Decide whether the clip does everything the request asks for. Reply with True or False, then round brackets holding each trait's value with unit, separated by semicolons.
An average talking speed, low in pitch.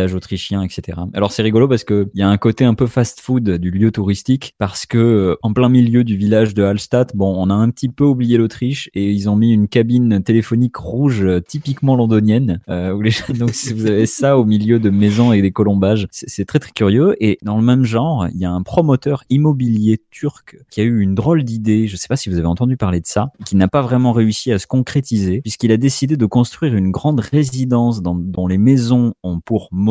False (230 wpm; 110 Hz)